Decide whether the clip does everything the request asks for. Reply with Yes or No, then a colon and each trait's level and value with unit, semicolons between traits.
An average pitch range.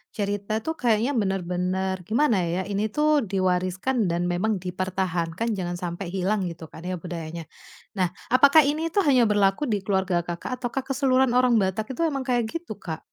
No: wide, 5.7 semitones